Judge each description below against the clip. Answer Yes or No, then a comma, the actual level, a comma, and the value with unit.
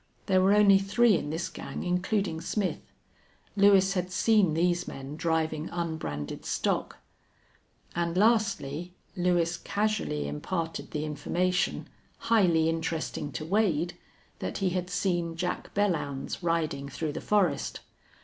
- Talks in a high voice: No, medium, 175 Hz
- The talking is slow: Yes, slow, 125 wpm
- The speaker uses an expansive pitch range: No, average, 3.3 semitones